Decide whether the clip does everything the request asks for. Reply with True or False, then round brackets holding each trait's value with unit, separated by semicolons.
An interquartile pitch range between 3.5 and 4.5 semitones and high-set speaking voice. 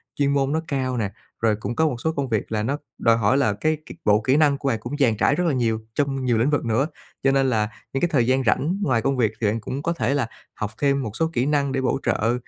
False (3.8 semitones; 130 Hz)